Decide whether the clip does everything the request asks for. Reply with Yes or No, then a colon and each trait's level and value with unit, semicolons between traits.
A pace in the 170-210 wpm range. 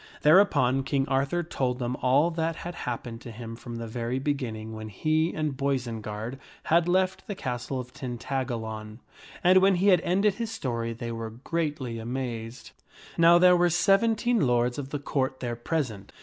Yes: average, 175 wpm